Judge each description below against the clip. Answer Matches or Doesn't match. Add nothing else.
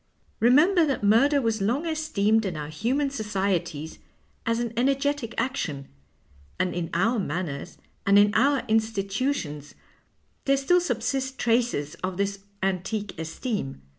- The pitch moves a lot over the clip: Matches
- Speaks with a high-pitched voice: Matches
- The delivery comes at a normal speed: Doesn't match